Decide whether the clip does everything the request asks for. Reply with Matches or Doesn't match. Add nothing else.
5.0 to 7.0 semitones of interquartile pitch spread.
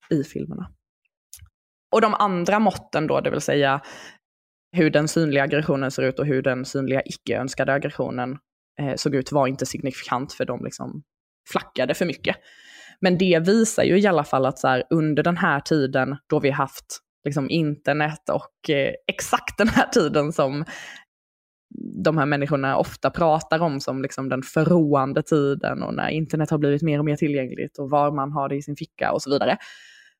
Doesn't match